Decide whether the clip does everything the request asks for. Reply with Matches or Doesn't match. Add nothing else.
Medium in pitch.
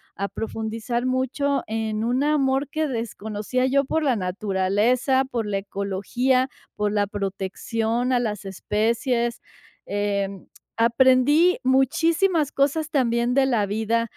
Doesn't match